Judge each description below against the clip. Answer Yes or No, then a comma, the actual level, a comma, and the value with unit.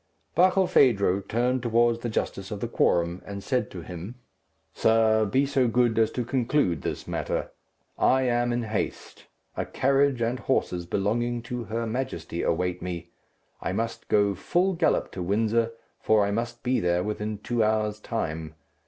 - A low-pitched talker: Yes, low, 115 Hz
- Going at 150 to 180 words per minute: Yes, average, 160 wpm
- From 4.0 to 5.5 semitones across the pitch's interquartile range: No, average, 3.5 semitones